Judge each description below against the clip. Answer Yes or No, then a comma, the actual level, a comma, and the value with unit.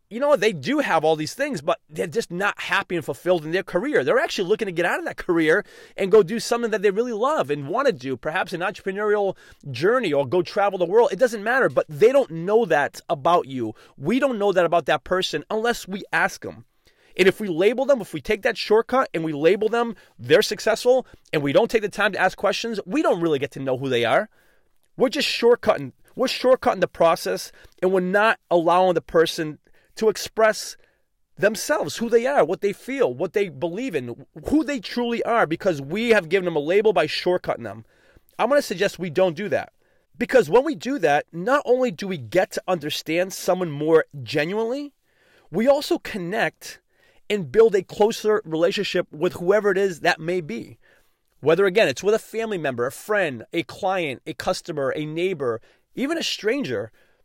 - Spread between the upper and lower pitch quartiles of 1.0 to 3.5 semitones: No, average, 5.2 semitones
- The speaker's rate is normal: No, fast, 210 wpm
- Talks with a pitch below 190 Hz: No, high, 195 Hz